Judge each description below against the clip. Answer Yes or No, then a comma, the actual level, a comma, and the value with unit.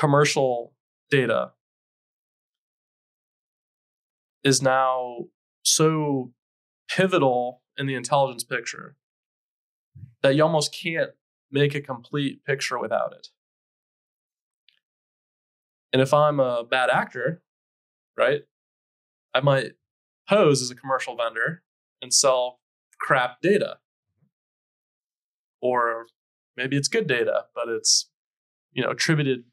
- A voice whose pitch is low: Yes, low, 130 Hz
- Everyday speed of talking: No, slow, 100 wpm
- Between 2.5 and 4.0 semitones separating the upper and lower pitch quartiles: Yes, average, 3.4 semitones